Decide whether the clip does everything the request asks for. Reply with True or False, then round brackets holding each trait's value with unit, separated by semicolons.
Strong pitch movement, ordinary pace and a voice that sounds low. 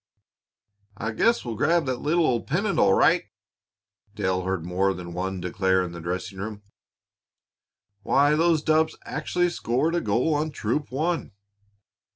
True (8.8 semitones; 150 wpm; 115 Hz)